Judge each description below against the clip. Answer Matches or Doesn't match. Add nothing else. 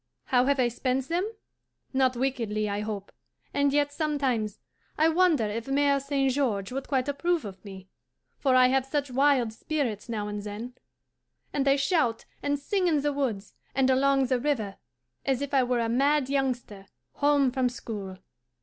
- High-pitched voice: Matches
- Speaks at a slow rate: Doesn't match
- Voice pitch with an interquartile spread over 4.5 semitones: Doesn't match